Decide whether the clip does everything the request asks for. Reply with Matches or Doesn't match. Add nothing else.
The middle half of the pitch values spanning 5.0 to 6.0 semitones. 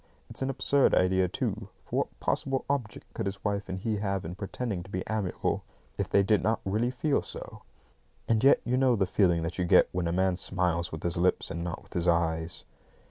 Doesn't match